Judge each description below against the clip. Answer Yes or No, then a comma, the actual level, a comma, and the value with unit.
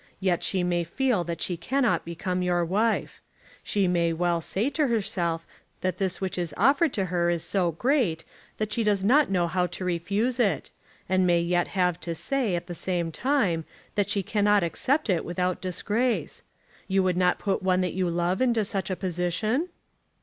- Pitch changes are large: No, average, 3.4 semitones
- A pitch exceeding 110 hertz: Yes, medium, 185 Hz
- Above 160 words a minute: Yes, average, 190 wpm